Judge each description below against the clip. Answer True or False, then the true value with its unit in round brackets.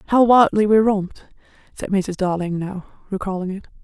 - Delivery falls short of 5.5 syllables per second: True (4.9 syllables/s)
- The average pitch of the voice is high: True (195 Hz)